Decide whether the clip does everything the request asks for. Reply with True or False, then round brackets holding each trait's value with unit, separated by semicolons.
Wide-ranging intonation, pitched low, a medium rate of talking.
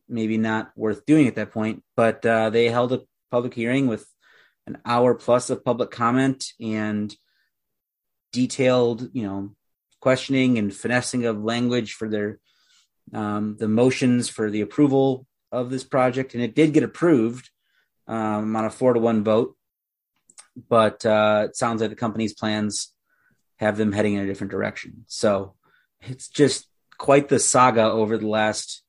False (2.9 semitones; 115 Hz; 160 wpm)